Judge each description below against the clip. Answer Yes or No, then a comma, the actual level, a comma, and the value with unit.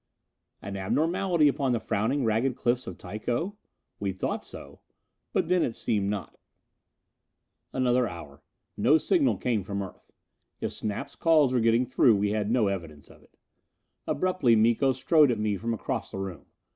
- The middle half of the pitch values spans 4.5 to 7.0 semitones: Yes, average, 5.1 semitones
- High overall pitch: No, low, 115 Hz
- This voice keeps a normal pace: Yes, average, 160 wpm